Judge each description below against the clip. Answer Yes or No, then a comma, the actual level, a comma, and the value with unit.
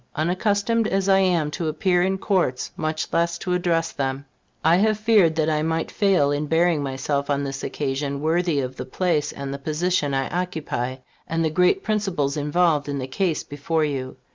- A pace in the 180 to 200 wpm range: Yes, average, 190 wpm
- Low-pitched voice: No, medium, 160 Hz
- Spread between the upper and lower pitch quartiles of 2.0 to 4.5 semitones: Yes, average, 4.0 semitones